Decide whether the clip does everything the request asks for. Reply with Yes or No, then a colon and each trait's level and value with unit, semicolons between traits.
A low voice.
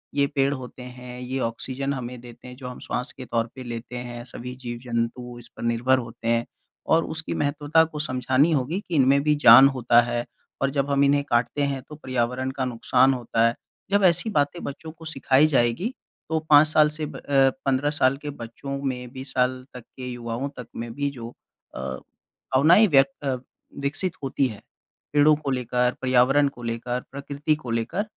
Yes: low, 130 Hz